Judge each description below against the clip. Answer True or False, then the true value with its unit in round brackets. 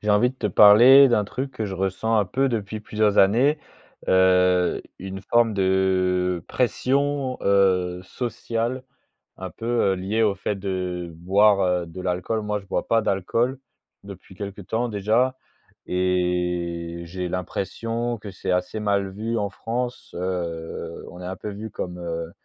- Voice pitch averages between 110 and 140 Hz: False (100 Hz)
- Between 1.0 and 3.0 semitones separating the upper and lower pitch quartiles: False (3.7 semitones)